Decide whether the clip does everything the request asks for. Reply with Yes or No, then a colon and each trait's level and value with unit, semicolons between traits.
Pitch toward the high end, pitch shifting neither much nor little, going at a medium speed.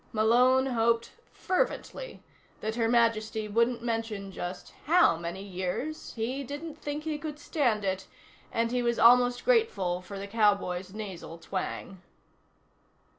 No: high, 230 Hz; average, 4.6 semitones; slow, 130 wpm